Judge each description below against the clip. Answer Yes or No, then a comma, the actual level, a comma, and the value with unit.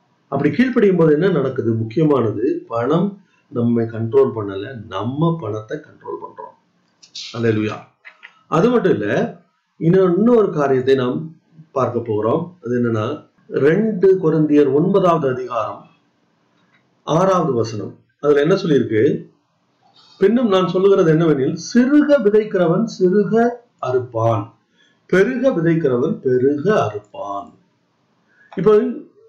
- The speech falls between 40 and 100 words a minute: Yes, average, 80 wpm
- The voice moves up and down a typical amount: No, wide, 8.9 semitones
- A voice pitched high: No, medium, 160 Hz